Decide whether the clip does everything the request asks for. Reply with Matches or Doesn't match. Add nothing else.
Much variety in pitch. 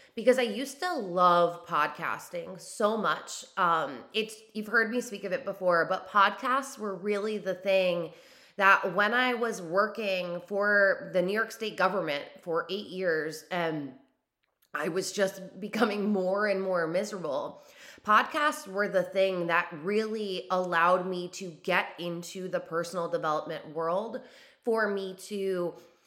Doesn't match